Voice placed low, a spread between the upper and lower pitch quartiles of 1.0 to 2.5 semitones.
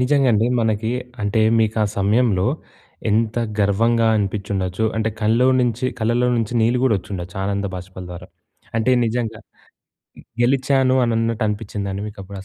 No: low, 110 Hz; average, 2.9 semitones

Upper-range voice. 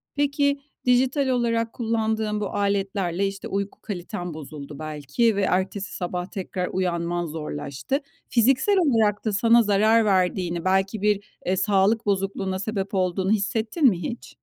Yes: high, 200 Hz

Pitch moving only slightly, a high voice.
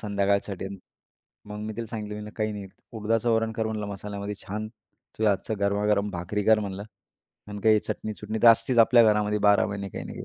No: narrow, 1.4 semitones; low, 105 Hz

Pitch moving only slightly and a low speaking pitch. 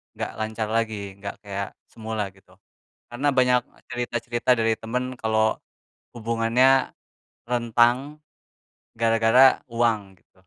Yes: narrow, 2.0 semitones; low, 115 Hz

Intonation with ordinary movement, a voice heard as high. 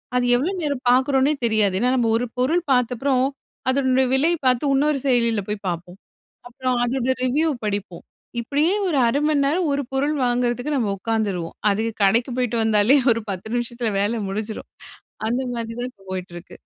Yes: average, 3.6 semitones; high, 245 Hz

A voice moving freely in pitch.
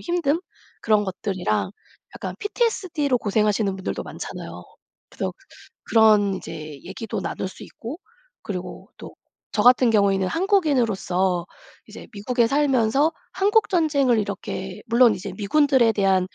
Yes: wide, 6.6 semitones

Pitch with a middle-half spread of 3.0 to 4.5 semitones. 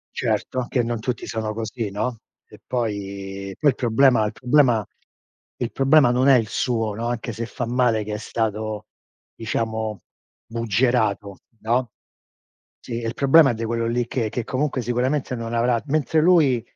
No: narrow, 2.5 semitones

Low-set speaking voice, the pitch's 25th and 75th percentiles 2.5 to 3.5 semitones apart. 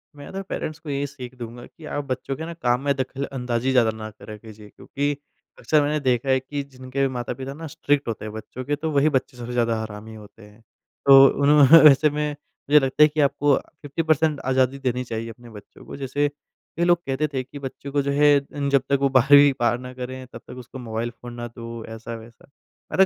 Yes: low, 130 Hz; average, 3.2 semitones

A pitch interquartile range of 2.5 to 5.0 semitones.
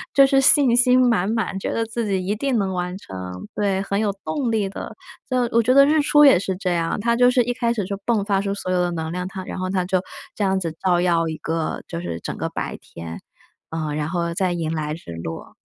No: wide, 5.4 semitones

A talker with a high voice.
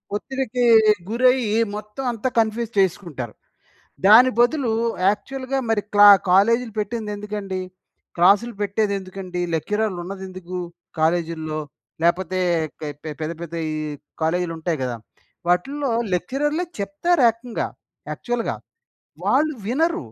Yes: high, 210 Hz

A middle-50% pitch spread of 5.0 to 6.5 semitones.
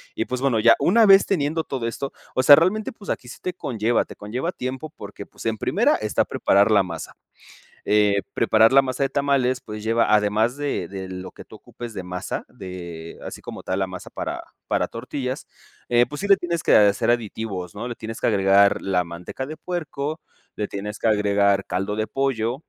Yes: average, 5.3 semitones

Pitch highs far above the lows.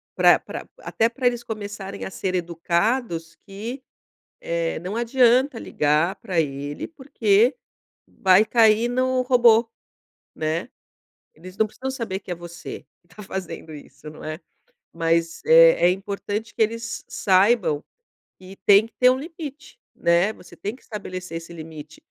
Yes: wide, 5.7 semitones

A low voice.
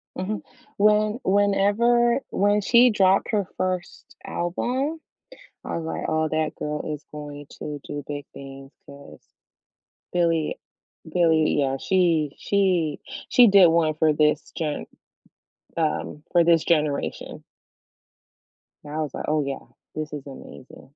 No: medium, 165 Hz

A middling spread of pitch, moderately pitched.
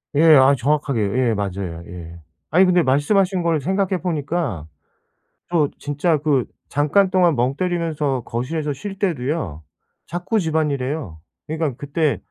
Yes: average, 4.9 semitones; medium, 150 Hz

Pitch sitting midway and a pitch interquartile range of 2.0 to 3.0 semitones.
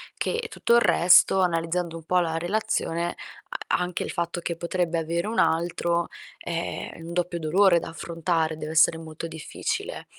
No: medium, 170 Hz; narrow, 1.4 semitones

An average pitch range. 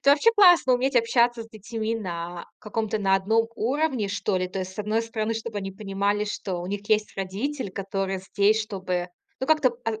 Yes: average, 3.0 semitones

